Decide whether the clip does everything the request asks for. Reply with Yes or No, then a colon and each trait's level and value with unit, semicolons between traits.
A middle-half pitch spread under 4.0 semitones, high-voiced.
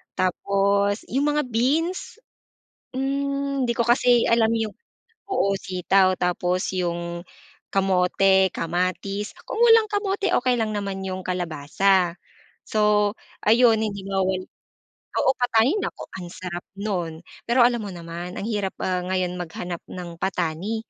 No: average, 4.6 semitones; high, 195 Hz